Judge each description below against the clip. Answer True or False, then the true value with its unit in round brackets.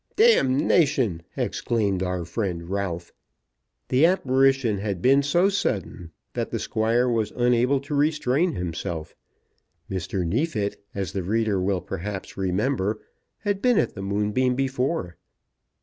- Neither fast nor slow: False (130 wpm)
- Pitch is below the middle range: True (110 Hz)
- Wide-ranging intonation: True (6.1 semitones)